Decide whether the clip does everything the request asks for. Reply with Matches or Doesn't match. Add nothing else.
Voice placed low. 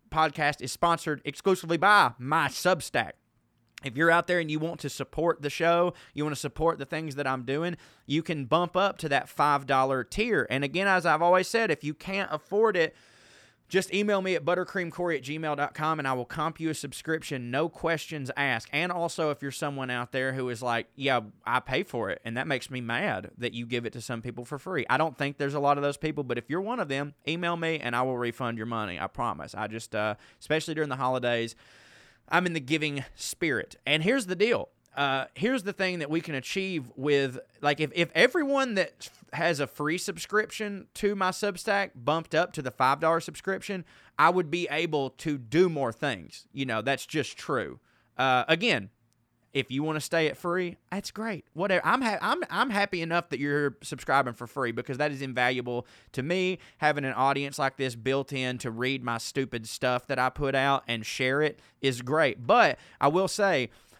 Doesn't match